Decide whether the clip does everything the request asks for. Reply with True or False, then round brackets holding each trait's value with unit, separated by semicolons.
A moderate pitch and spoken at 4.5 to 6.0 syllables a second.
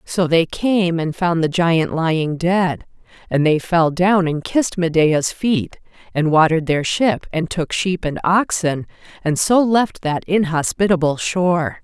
False (170 Hz; 4.1 syllables/s)